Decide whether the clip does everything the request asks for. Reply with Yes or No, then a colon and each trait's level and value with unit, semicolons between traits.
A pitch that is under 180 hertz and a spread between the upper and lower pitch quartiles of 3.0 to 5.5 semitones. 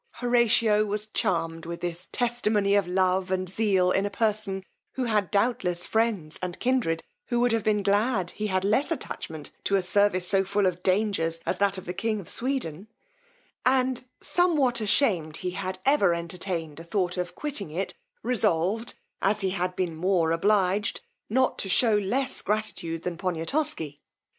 No: high, 195 Hz; average, 3.7 semitones